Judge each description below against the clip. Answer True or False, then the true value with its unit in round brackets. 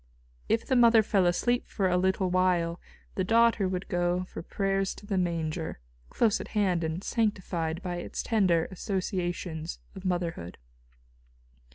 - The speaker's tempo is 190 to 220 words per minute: False (150 wpm)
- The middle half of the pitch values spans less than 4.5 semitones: True (2.5 semitones)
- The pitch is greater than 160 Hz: True (185 Hz)